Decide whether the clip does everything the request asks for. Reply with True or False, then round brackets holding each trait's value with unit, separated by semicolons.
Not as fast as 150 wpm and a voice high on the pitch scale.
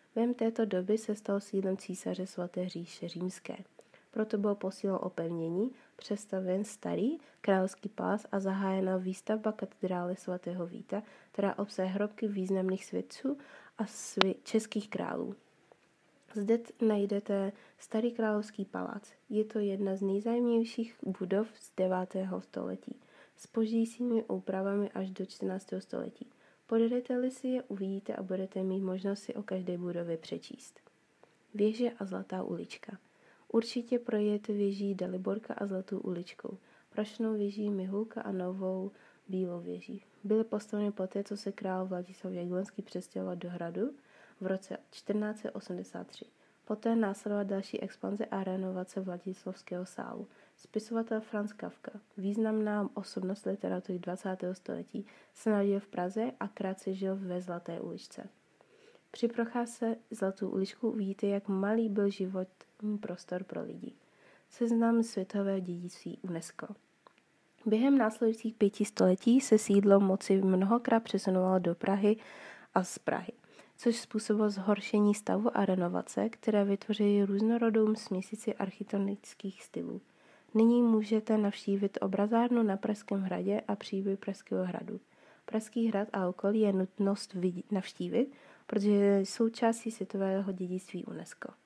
True (125 wpm; 200 Hz)